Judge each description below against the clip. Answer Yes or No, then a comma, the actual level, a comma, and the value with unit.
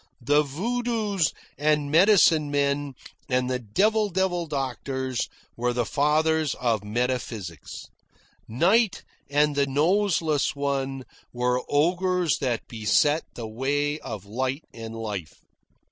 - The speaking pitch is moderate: Yes, medium, 145 Hz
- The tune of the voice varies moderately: Yes, average, 4.6 semitones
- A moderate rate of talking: No, slow, 115 wpm